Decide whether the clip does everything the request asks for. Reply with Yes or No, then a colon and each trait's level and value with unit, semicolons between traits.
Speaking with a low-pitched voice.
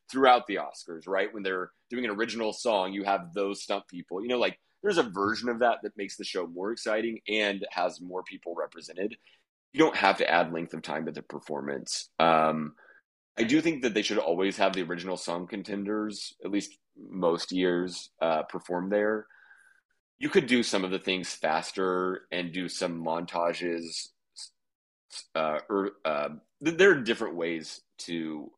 Yes: very low, 95 Hz